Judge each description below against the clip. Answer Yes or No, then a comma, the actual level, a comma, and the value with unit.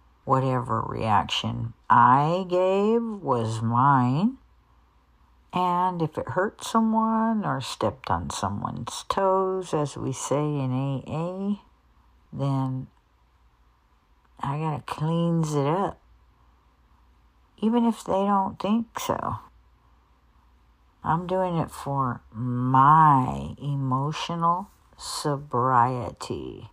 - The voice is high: No, low, 135 Hz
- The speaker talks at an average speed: No, slow, 90 wpm